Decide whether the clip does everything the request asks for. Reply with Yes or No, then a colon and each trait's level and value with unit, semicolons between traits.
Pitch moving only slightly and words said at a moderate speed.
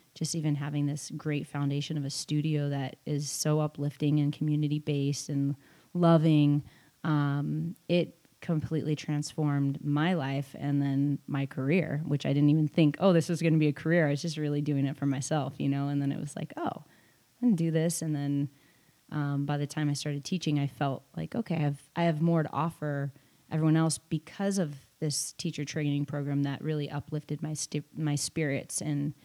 Yes: narrow, 1.8 semitones; average, 195 wpm